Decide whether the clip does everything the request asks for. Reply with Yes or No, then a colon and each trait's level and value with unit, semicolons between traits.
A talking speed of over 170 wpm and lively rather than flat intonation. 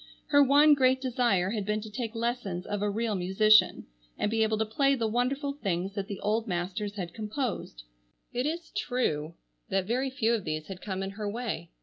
No: fast, 205 wpm; average, 4.3 semitones